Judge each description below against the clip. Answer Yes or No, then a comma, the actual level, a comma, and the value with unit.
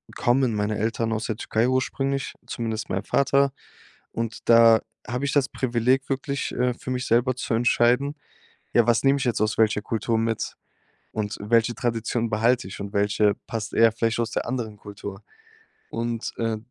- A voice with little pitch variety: Yes, narrow, 2.3 semitones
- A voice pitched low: Yes, low, 115 Hz